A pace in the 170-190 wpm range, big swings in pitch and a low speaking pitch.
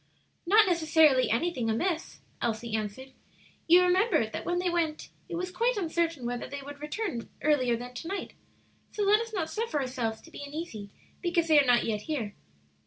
No: average, 180 wpm; wide, 6.4 semitones; very high, 310 Hz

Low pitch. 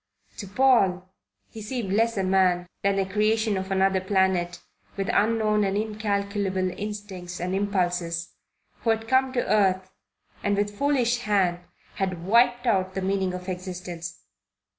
No: high, 195 Hz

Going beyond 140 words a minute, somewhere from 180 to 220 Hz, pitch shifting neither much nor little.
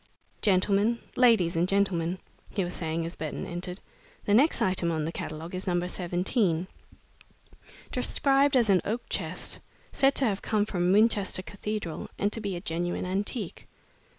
Yes: average, 155 wpm; high, 190 Hz; average, 3.3 semitones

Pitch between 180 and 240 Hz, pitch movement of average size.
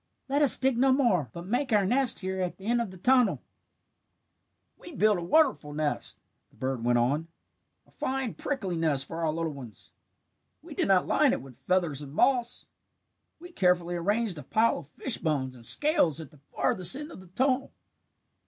No: medium, 185 Hz; wide, 8.5 semitones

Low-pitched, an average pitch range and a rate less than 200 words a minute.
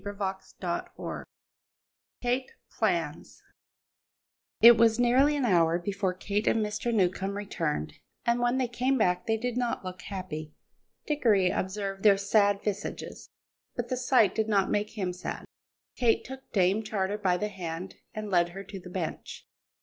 No: high, 205 Hz; average, 3.8 semitones; average, 155 wpm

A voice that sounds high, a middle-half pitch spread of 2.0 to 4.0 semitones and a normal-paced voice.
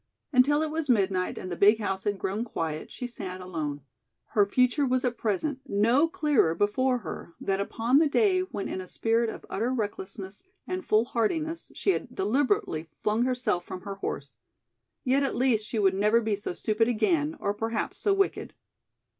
No: high, 225 Hz; average, 5.0 semitones; average, 180 wpm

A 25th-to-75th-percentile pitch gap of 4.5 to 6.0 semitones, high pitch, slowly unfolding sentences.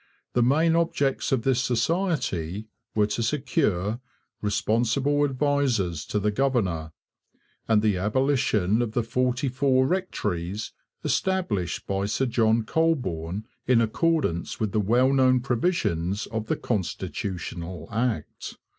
No: average, 5.0 semitones; low, 115 Hz; slow, 120 wpm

